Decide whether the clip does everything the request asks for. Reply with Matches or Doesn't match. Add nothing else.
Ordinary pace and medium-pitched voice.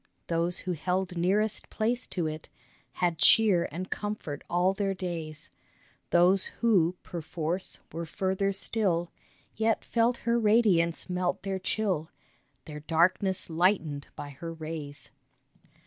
Doesn't match